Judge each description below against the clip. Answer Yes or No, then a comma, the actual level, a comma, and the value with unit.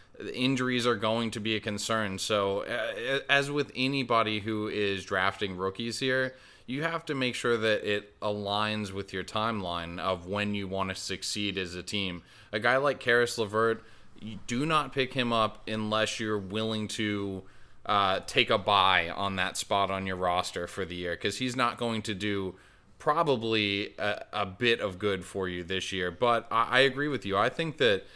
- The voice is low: Yes, low, 105 Hz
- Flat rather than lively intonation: No, average, 3.6 semitones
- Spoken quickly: No, average, 190 wpm